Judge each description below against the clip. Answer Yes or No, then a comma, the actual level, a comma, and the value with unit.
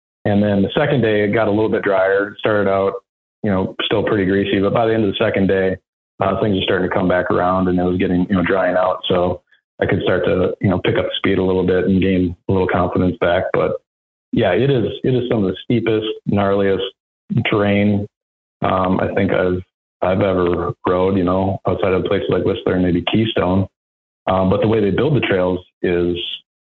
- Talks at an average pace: No, fast, 225 wpm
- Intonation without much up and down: Yes, narrow, 2.1 semitones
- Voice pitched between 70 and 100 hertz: Yes, very low, 95 Hz